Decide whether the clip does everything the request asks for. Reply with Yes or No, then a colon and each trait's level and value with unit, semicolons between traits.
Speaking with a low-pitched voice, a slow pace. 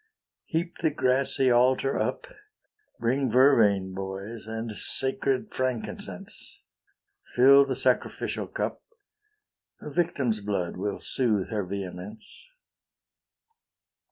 Yes: low, 120 Hz; slow, 95 wpm